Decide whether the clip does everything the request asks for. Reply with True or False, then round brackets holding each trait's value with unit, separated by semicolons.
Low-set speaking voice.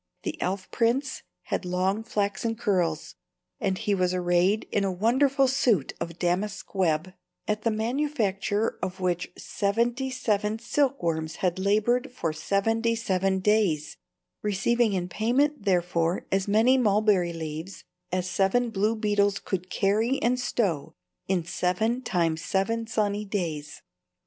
False (200 Hz)